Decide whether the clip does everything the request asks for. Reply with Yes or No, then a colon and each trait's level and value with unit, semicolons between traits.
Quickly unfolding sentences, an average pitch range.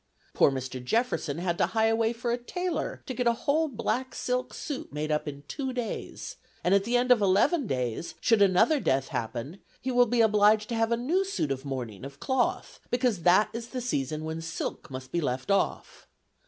No: fast, 210 wpm; wide, 8.6 semitones